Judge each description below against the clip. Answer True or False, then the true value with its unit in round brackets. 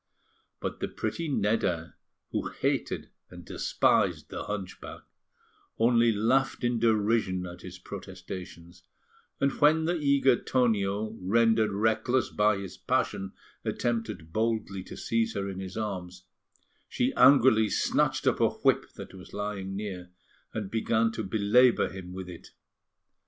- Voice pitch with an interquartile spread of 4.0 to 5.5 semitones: False (3.5 semitones)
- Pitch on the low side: True (105 Hz)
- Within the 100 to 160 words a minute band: True (135 wpm)